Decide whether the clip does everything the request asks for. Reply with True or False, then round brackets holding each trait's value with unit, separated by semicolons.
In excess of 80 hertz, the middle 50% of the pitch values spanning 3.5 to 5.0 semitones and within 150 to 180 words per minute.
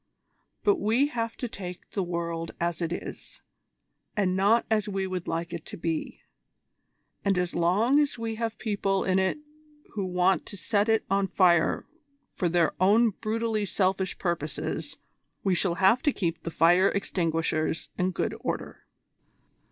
True (190 Hz; 3.8 semitones; 160 wpm)